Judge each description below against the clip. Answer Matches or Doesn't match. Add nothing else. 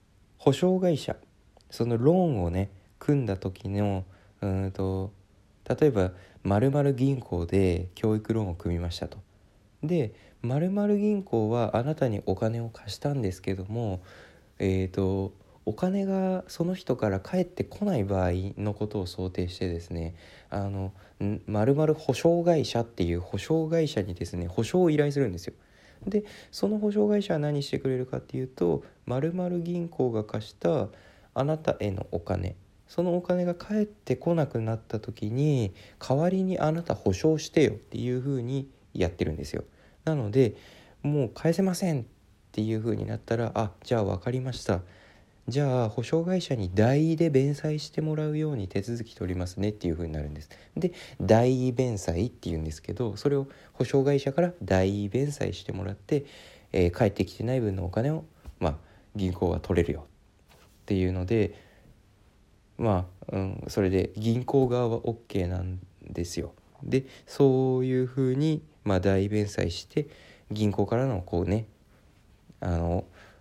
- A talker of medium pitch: Doesn't match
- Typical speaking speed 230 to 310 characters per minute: Matches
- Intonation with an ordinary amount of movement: Doesn't match